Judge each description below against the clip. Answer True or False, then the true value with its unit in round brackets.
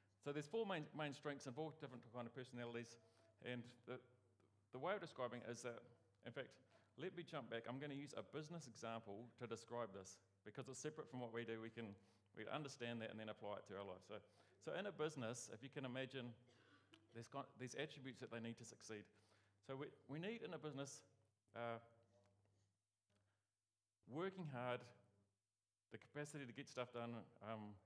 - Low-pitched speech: True (120 Hz)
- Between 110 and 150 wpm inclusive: False (195 wpm)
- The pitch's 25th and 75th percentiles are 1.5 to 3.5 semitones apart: False (4.1 semitones)